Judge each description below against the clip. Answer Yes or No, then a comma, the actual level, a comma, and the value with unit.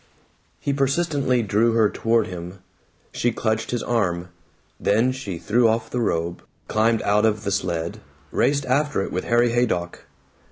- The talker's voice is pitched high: No, low, 115 Hz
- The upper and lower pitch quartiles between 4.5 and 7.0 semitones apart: No, average, 3.9 semitones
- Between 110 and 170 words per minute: Yes, average, 155 wpm